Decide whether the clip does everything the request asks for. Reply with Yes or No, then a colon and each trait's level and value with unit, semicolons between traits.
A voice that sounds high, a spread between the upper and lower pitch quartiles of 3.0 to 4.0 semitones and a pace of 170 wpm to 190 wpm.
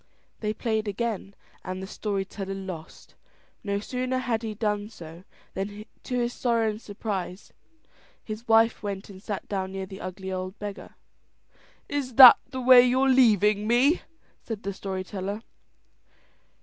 No: high, 210 Hz; average, 3.4 semitones; average, 150 wpm